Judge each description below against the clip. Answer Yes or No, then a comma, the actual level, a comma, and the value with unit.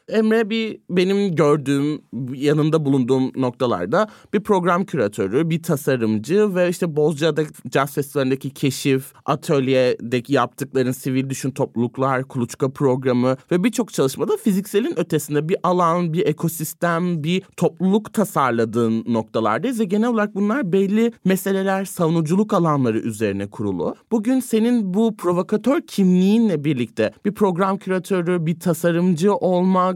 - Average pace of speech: Yes, average, 120 wpm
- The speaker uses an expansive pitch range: Yes, wide, 6.5 semitones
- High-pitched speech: No, medium, 165 Hz